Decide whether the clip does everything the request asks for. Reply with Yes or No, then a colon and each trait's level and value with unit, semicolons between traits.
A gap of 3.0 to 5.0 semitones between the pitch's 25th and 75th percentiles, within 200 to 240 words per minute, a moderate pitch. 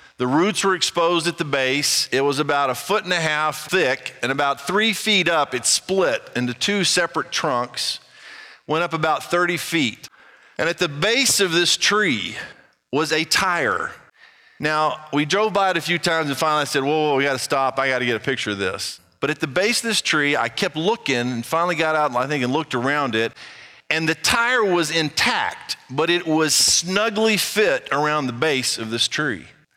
Yes: average, 4.2 semitones; fast, 205 wpm; medium, 155 Hz